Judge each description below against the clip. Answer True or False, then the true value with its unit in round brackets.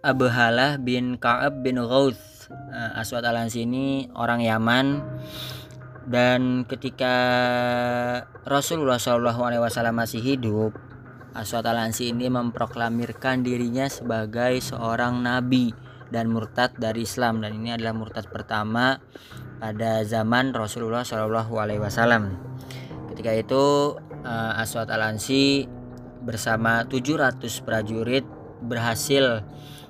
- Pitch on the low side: True (120 Hz)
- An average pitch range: False (2.1 semitones)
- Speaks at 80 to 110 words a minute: True (90 wpm)